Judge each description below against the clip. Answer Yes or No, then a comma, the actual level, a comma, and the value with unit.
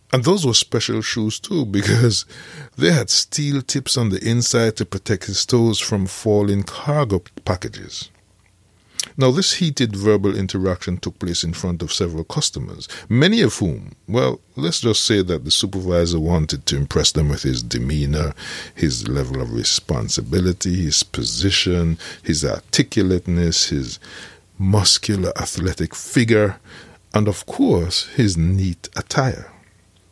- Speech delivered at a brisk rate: No, slow, 135 wpm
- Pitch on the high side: No, very low, 95 Hz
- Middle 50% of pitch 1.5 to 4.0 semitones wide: No, average, 4.5 semitones